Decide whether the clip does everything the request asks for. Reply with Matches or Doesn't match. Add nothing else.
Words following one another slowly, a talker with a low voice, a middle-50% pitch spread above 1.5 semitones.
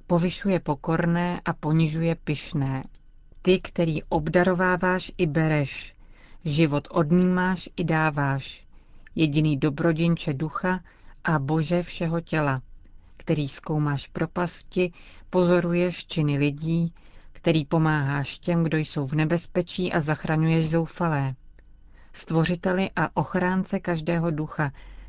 Doesn't match